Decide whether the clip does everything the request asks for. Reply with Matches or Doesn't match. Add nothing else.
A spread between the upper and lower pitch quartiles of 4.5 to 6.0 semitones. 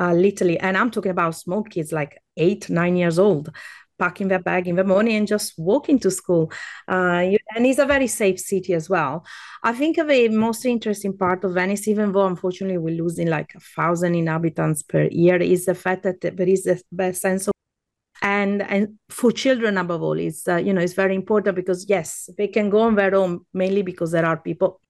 Doesn't match